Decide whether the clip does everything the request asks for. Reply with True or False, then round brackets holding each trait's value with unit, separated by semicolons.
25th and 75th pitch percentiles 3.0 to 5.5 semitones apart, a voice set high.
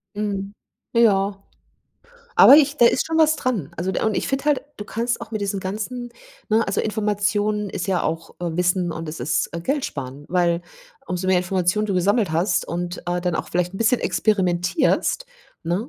True (3.8 semitones; 195 Hz)